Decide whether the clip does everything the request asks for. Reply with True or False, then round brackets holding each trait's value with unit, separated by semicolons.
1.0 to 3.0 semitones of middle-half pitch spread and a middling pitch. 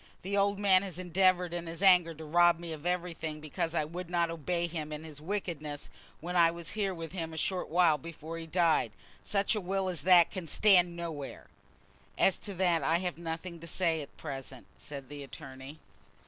True (2.4 semitones; 170 Hz)